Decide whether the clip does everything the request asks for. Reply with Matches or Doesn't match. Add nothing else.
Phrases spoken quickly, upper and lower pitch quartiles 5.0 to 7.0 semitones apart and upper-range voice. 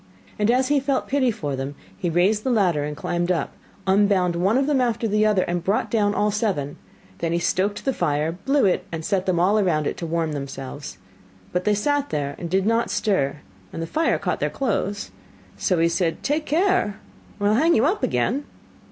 Matches